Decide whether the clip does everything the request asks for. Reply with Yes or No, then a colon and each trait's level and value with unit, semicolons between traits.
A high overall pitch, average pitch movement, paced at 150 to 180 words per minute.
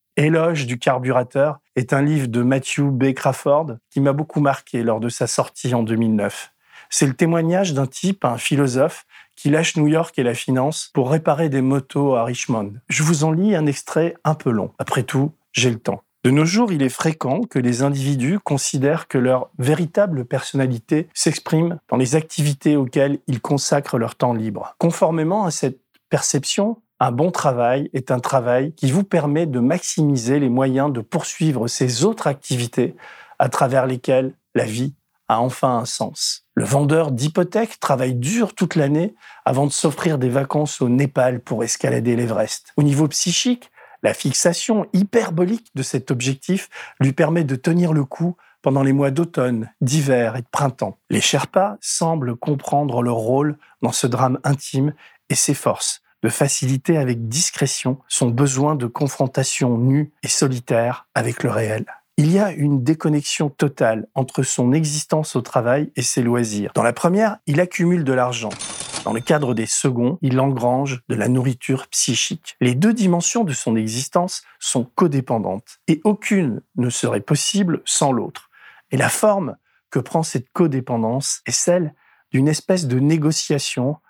No: medium, 140 Hz; average, 3.9 semitones; average, 170 wpm